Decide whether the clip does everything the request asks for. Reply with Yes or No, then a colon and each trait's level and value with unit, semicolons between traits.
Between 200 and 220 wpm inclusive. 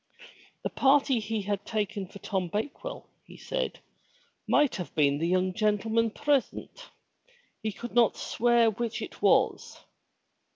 No: slow, 135 wpm